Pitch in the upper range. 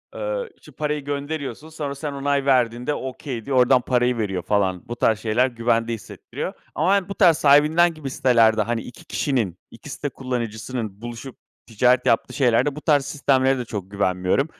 No: low, 130 Hz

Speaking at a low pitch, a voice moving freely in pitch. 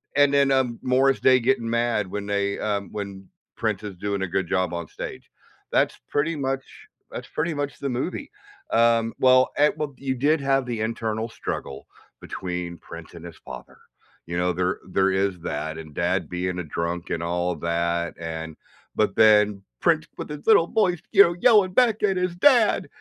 Yes: low, 110 Hz; wide, 7.6 semitones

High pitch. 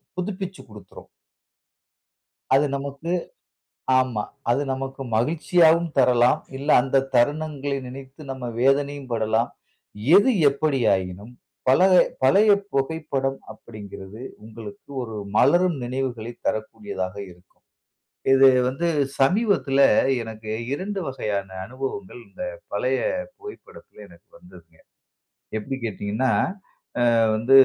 No: low, 135 Hz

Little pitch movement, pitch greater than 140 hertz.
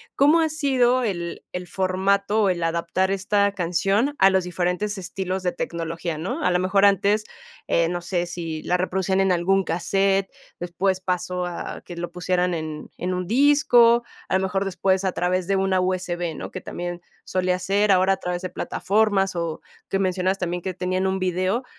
Yes: narrow, 1.8 semitones; medium, 185 Hz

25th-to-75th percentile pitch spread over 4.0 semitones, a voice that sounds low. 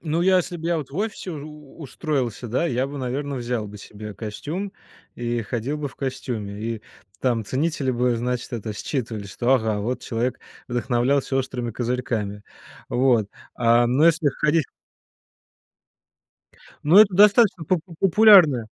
Yes: average, 4.7 semitones; low, 130 Hz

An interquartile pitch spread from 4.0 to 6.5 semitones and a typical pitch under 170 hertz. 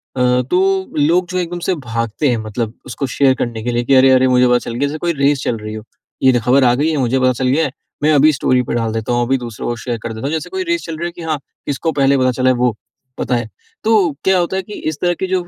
Yes: average, 5.0 semitones; low, 135 Hz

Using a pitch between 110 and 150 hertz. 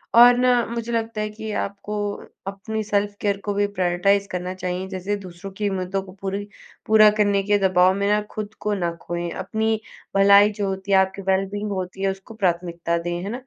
No: high, 200 Hz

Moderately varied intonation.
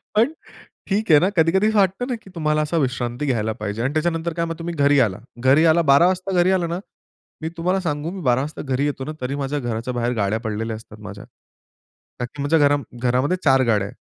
No: wide, 5.7 semitones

